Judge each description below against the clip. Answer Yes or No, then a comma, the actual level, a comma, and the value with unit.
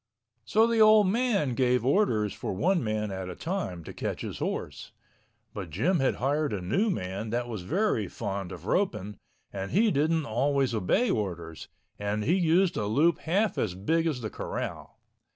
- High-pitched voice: No, low, 125 Hz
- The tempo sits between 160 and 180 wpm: Yes, average, 175 wpm